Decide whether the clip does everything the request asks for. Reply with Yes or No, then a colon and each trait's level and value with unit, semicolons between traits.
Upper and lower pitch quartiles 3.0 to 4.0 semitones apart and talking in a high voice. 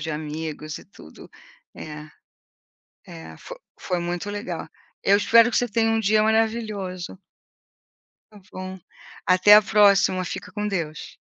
No: average, 4.7 semitones; high, 195 Hz